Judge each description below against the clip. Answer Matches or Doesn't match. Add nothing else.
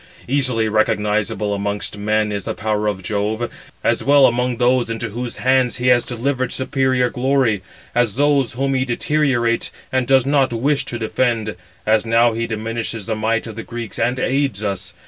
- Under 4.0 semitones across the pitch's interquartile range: Matches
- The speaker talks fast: Doesn't match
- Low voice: Matches